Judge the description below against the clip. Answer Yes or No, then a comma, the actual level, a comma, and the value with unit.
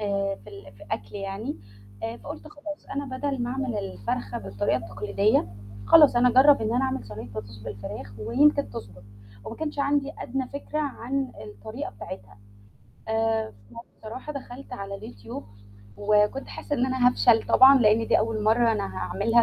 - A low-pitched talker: No, high, 225 Hz